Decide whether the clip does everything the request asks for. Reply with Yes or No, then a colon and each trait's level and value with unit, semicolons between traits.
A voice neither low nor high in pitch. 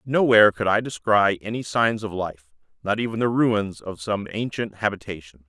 No: low, 105 Hz